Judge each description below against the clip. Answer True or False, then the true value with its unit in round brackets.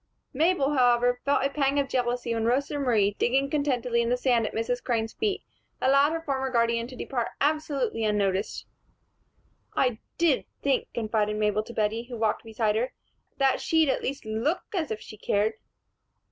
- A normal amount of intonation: True (3.8 semitones)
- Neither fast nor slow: True (175 wpm)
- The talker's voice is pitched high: True (245 Hz)